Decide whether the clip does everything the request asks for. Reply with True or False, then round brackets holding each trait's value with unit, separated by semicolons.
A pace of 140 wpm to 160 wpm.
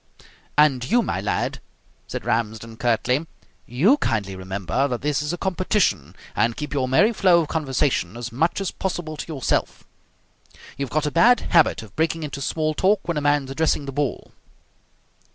False (170 wpm)